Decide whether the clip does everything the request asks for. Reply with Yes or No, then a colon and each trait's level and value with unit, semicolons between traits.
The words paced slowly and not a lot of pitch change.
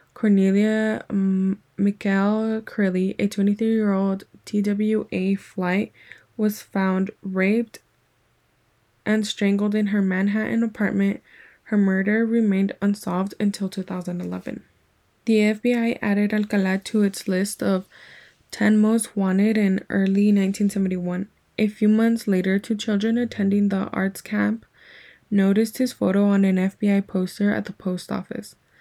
Yes: slow, 120 wpm; narrow, 1.8 semitones